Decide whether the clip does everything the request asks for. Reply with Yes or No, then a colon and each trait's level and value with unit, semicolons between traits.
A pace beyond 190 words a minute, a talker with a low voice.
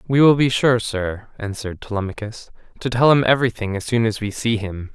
Yes: fast, 205 wpm; low, 115 Hz